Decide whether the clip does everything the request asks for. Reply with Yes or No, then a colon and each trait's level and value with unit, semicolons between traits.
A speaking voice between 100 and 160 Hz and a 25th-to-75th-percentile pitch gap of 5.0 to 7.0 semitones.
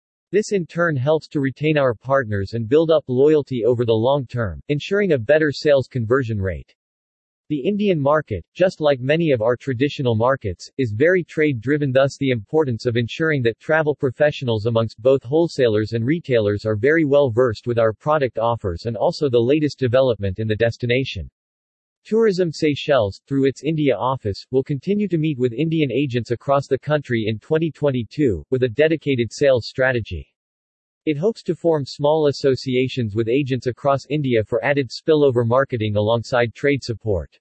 No: low, 135 Hz; average, 4.4 semitones